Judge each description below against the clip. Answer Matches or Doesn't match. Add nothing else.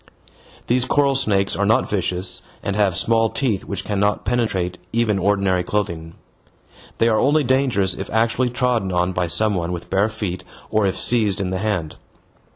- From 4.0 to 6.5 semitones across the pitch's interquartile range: Doesn't match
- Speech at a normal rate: Matches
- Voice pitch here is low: Matches